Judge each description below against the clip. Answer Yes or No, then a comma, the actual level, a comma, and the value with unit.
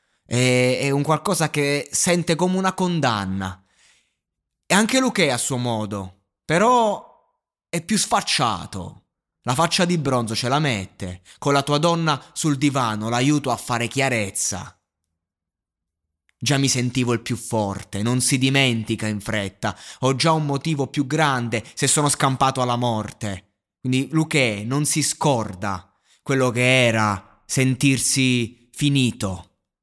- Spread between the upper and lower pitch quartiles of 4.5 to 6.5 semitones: Yes, wide, 5.5 semitones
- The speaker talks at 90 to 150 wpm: Yes, average, 135 wpm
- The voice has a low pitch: Yes, low, 125 Hz